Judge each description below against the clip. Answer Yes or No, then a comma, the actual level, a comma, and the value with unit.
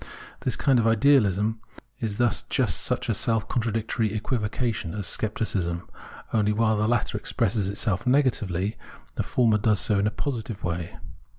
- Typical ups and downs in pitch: No, narrow, 2.2 semitones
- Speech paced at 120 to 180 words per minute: Yes, average, 155 wpm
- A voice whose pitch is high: No, low, 110 Hz